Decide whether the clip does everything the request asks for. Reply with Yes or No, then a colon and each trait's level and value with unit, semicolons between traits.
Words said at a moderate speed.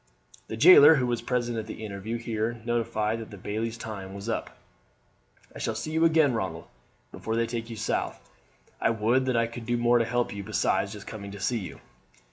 No: fast, 210 wpm